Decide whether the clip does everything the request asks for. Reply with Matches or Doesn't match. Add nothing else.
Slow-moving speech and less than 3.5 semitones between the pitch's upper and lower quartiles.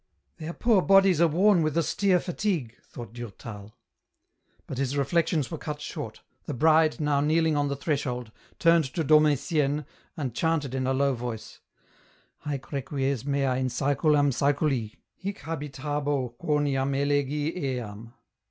Doesn't match